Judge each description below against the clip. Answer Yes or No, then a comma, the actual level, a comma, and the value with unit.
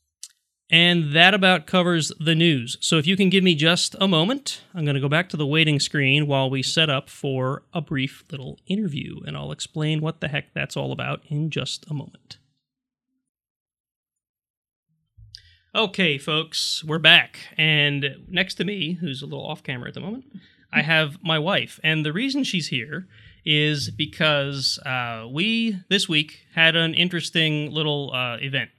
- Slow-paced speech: No, average, 175 wpm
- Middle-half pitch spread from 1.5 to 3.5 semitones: No, average, 4.0 semitones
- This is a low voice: No, medium, 155 Hz